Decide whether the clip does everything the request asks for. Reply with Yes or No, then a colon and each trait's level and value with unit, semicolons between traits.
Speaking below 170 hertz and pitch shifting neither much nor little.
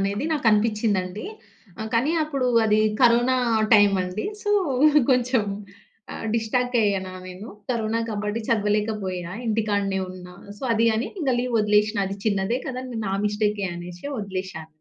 No: high, 210 Hz; average, 3.0 semitones